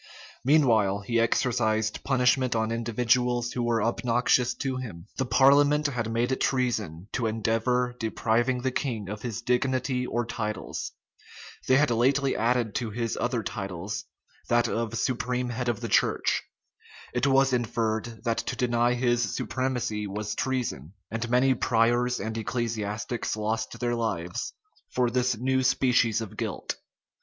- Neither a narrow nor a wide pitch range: No, narrow, 2.2 semitones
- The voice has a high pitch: No, low, 120 Hz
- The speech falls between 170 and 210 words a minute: No, average, 145 wpm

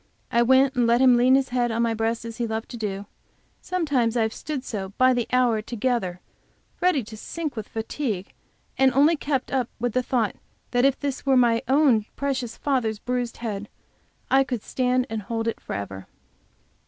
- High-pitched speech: Yes, high, 245 Hz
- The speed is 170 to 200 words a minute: Yes, average, 190 wpm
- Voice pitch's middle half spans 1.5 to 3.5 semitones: Yes, average, 2.9 semitones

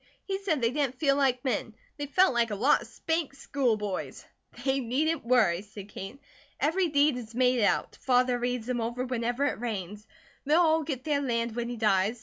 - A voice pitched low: No, very high, 250 Hz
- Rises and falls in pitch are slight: No, average, 3.7 semitones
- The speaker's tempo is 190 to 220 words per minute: Yes, average, 200 wpm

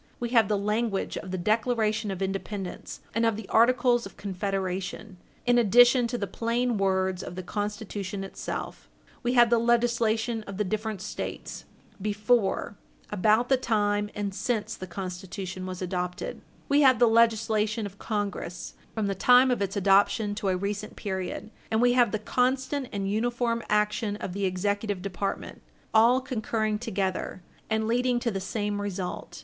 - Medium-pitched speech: No, high, 210 Hz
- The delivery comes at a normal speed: Yes, average, 165 wpm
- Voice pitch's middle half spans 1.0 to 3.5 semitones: Yes, average, 3.1 semitones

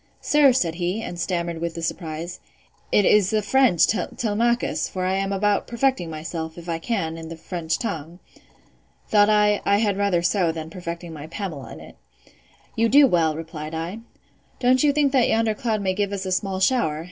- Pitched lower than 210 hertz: Yes, medium, 185 Hz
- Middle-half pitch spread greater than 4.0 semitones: Yes, average, 4.7 semitones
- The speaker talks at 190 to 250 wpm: No, average, 180 wpm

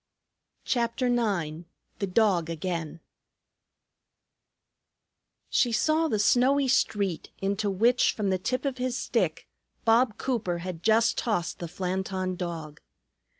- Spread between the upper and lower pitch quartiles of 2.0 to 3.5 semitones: No, average, 5.3 semitones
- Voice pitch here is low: No, high, 205 Hz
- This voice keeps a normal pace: No, slow, 115 wpm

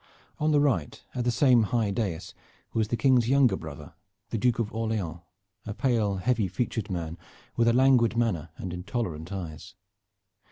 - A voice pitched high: No, low, 110 Hz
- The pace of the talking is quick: No, average, 165 wpm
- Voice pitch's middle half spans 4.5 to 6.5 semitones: Yes, average, 5.1 semitones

